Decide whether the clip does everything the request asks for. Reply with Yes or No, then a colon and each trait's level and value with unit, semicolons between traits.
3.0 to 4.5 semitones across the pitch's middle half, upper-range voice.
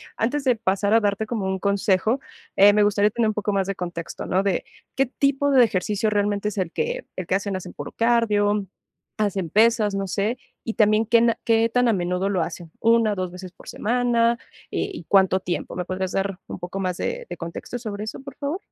Yes: average, 3.4 semitones; high, 205 Hz